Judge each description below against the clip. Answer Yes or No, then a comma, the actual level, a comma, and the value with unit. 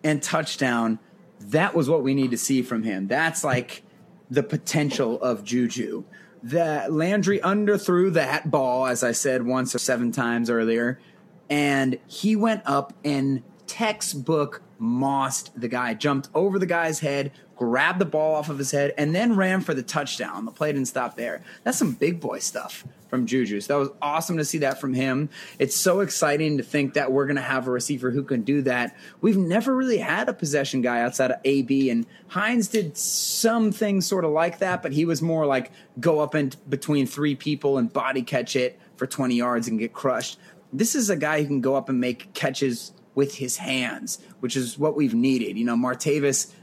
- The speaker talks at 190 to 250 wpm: Yes, average, 200 wpm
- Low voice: No, medium, 145 Hz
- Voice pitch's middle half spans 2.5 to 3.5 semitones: No, average, 4.7 semitones